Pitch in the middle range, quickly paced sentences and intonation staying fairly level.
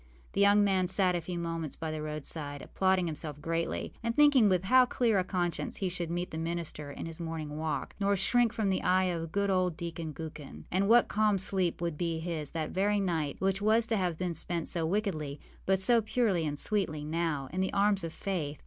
No: medium, 175 Hz; fast, 220 wpm; average, 3.6 semitones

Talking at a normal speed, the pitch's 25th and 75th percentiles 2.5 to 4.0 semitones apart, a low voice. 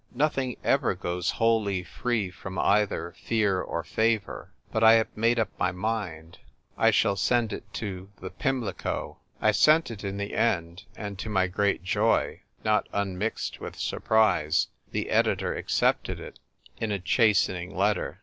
Yes: average, 160 wpm; average, 3.4 semitones; low, 100 Hz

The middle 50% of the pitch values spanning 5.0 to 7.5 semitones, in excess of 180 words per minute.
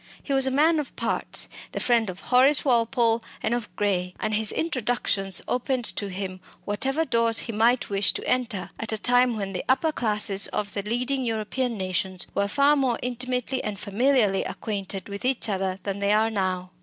No: average, 4.0 semitones; average, 190 wpm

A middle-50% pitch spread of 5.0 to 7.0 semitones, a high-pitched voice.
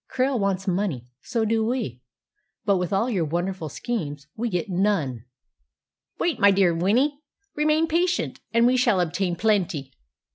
Yes: wide, 5.6 semitones; high, 200 Hz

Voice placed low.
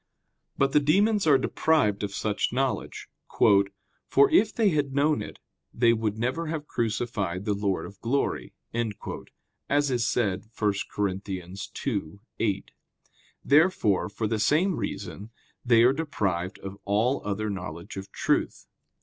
Yes: low, 115 Hz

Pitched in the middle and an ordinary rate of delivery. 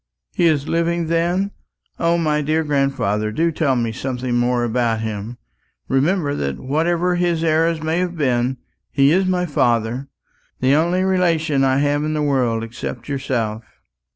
Yes: medium, 145 Hz; average, 155 wpm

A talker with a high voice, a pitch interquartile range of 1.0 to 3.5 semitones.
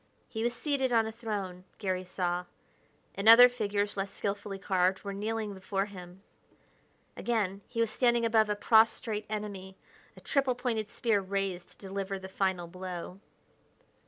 Yes: high, 200 Hz; average, 2.9 semitones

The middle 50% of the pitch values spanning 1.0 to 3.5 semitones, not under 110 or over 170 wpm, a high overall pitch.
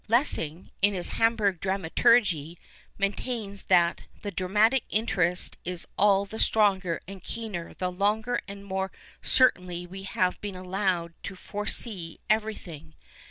Yes: average, 2.8 semitones; average, 145 wpm; high, 195 Hz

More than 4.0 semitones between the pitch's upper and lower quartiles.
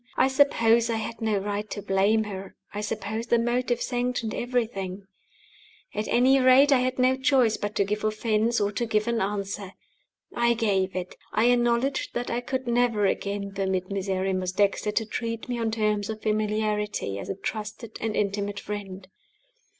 No: average, 3.0 semitones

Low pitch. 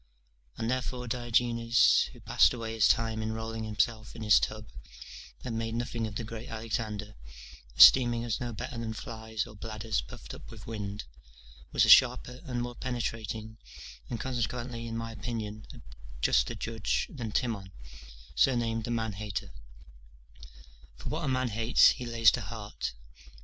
Yes: low, 115 Hz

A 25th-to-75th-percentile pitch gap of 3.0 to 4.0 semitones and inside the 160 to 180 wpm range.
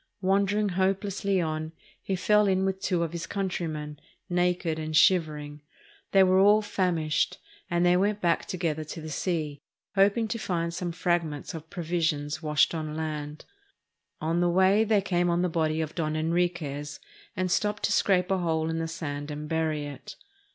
Yes: average, 3.3 semitones; average, 175 wpm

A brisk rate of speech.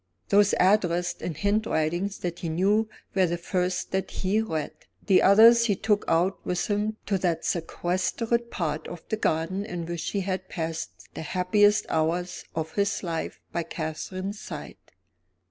No: average, 160 wpm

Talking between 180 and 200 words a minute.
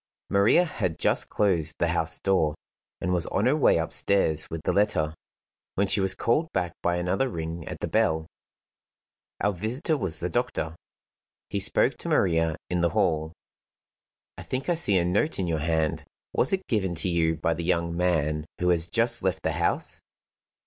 Yes: average, 185 wpm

